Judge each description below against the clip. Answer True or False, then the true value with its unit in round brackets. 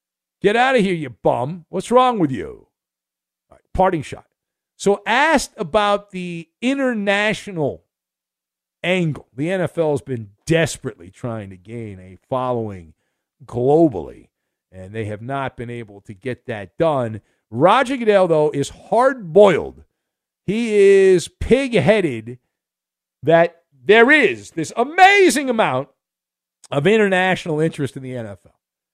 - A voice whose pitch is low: False (160 Hz)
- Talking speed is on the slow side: True (125 wpm)